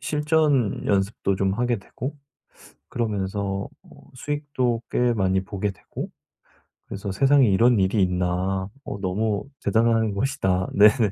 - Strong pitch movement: No, average, 4.2 semitones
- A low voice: Yes, low, 105 Hz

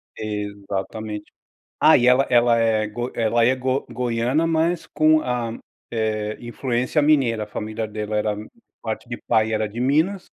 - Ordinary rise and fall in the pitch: Yes, average, 3.2 semitones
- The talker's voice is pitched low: Yes, low, 115 Hz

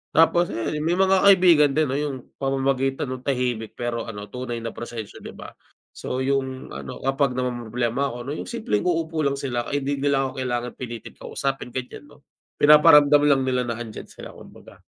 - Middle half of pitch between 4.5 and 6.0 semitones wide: No, average, 3.2 semitones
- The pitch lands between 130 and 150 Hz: Yes, low, 135 Hz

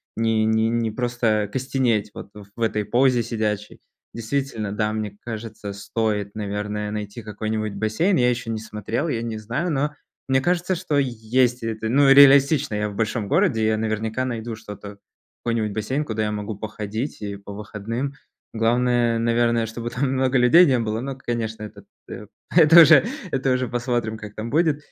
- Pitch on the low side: Yes, low, 115 Hz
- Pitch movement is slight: No, average, 3.1 semitones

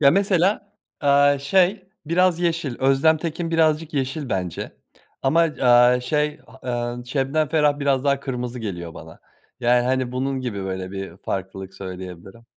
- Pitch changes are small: No, average, 4.7 semitones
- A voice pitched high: No, low, 135 Hz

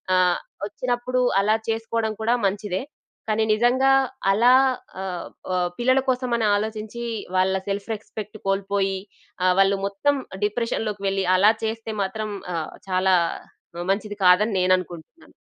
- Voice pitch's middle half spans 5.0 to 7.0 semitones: No, average, 2.9 semitones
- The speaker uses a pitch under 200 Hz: No, high, 210 Hz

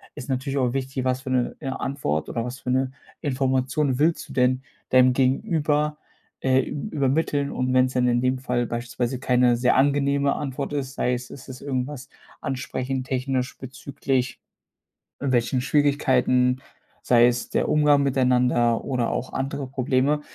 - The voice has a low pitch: Yes, low, 130 Hz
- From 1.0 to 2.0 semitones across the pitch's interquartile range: Yes, narrow, 1.7 semitones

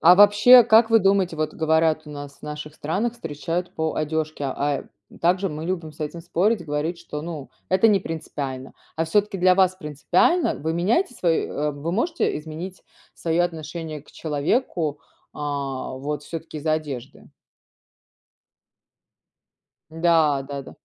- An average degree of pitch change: Yes, average, 3.5 semitones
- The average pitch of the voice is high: No, medium, 160 Hz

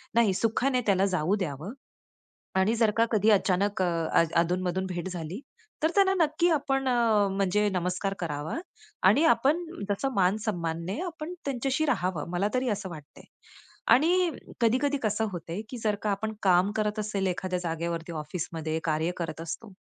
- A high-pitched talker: Yes, high, 195 Hz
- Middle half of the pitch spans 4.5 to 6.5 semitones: Yes, average, 4.9 semitones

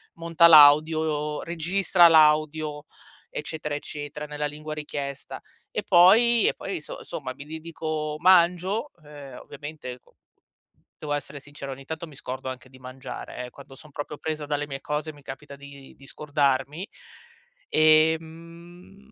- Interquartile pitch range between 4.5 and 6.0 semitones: No, narrow, 2.4 semitones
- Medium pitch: Yes, medium, 150 Hz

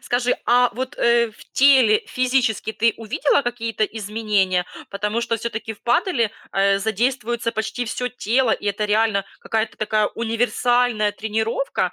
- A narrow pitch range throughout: Yes, narrow, 2.3 semitones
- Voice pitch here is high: Yes, high, 230 Hz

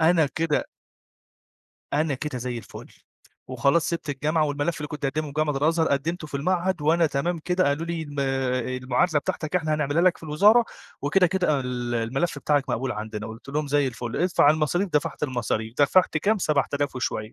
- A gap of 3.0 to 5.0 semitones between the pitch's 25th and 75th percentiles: Yes, average, 3.6 semitones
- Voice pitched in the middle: Yes, medium, 150 Hz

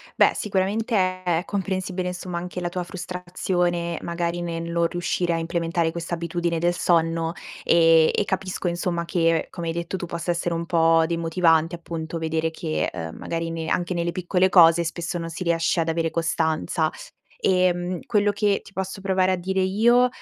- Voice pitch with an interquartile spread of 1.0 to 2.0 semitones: Yes, narrow, 1.7 semitones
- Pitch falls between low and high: Yes, medium, 170 Hz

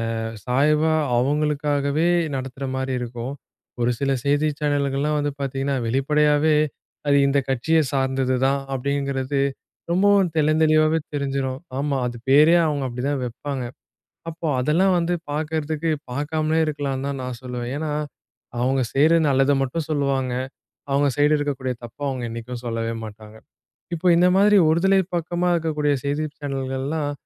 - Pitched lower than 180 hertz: Yes, medium, 140 Hz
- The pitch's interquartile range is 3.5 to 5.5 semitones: No, average, 2.7 semitones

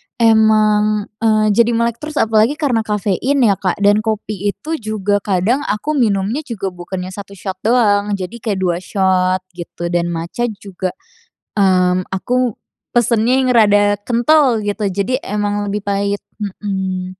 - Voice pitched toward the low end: No, high, 205 Hz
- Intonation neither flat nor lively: Yes, average, 3.1 semitones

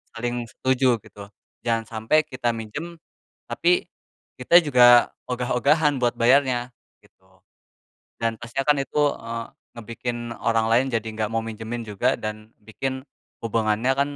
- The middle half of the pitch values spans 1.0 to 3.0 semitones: Yes, average, 2.7 semitones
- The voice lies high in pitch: No, low, 120 Hz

